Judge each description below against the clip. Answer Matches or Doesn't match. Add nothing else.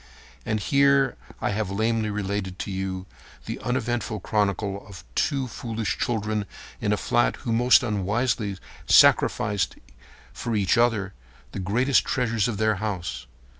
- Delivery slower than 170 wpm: Matches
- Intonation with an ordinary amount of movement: Matches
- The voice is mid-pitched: Doesn't match